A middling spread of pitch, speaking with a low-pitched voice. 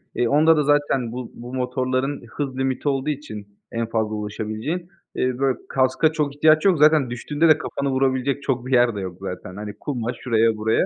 Yes: average, 4.2 semitones; low, 130 Hz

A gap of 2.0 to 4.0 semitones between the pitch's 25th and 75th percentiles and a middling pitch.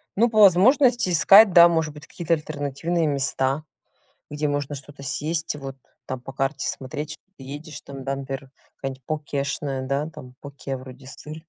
Yes: average, 2.9 semitones; medium, 145 Hz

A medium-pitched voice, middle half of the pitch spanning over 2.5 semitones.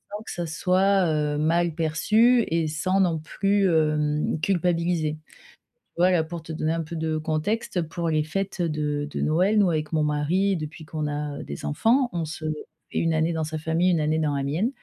Yes: medium, 160 Hz; average, 2.9 semitones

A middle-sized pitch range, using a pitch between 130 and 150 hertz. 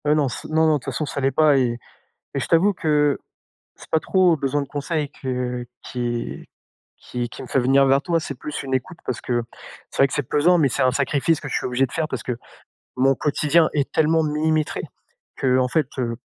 Yes: average, 3.2 semitones; medium, 140 Hz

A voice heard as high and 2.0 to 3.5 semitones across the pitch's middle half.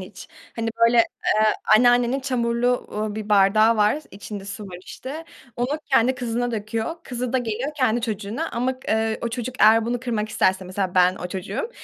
Yes: high, 230 Hz; average, 2.9 semitones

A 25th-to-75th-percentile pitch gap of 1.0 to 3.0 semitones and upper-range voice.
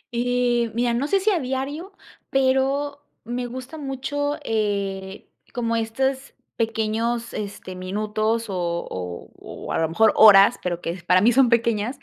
No: average, 4.5 semitones; high, 235 Hz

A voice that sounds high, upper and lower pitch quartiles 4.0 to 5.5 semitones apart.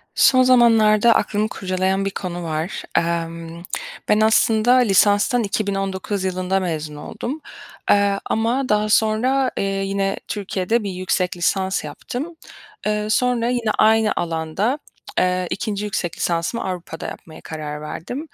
No: high, 200 Hz; average, 3.6 semitones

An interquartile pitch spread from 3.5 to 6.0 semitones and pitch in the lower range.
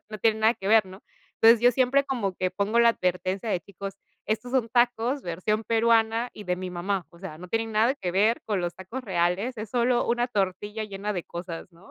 No: average, 3.9 semitones; high, 215 Hz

